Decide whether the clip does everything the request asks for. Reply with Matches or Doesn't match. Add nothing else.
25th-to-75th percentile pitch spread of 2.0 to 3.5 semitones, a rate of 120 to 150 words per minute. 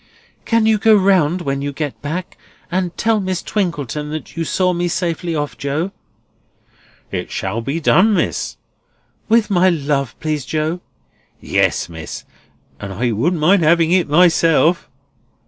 Doesn't match